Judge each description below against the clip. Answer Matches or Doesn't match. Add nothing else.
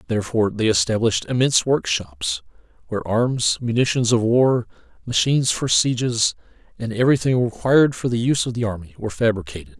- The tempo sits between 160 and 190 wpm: Doesn't match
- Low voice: Matches